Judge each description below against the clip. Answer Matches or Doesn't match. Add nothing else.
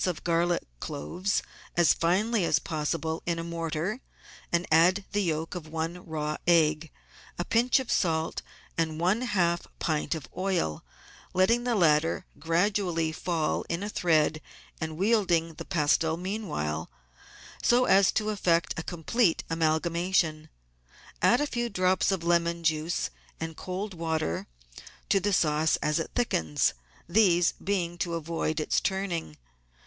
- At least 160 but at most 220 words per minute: Doesn't match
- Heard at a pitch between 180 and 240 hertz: Doesn't match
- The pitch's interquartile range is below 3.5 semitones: Matches